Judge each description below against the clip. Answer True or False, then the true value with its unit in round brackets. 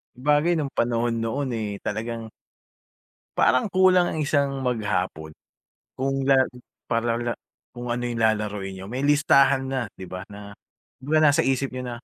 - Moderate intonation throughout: True (3.7 semitones)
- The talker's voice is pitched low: True (120 Hz)